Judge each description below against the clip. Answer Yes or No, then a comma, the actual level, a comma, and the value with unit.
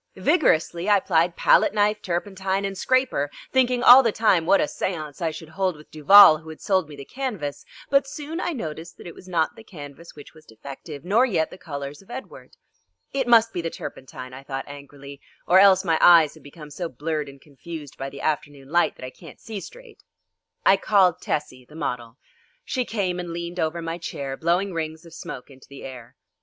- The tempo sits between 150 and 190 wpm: No, fast, 205 wpm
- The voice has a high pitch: No, medium, 170 Hz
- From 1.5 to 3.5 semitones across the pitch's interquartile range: No, average, 5.3 semitones